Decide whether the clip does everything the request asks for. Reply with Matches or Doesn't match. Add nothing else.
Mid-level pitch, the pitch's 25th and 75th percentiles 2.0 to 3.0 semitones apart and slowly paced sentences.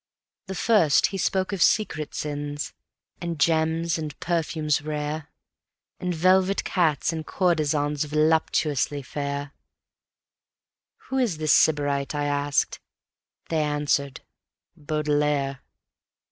Matches